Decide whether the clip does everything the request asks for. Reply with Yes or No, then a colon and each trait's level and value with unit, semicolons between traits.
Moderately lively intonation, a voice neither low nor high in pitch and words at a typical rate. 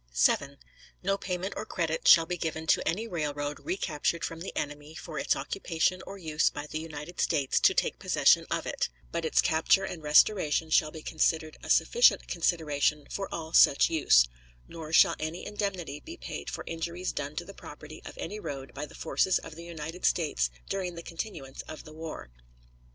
Yes: average, 3.1 semitones; medium, 160 Hz; average, 190 wpm